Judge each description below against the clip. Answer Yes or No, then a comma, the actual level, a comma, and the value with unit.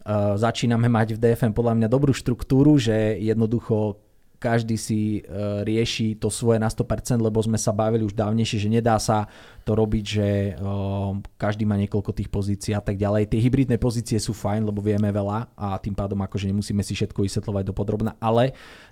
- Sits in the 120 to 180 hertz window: No, low, 110 Hz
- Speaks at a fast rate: Yes, fast, 180 wpm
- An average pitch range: No, narrow, 1.9 semitones